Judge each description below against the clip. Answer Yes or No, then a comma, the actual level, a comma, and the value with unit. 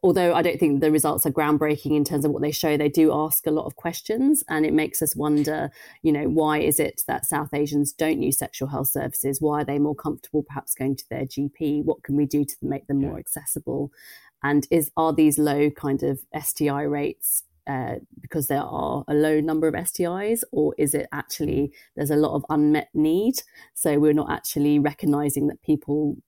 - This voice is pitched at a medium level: Yes, medium, 150 Hz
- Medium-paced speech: No, fast, 210 wpm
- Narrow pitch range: Yes, narrow, 1.3 semitones